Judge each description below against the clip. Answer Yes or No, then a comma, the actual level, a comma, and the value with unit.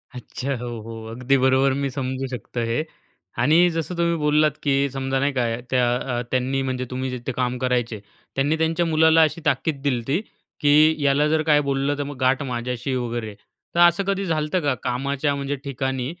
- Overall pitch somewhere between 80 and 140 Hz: Yes, low, 135 Hz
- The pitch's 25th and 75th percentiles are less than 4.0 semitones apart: Yes, average, 3.0 semitones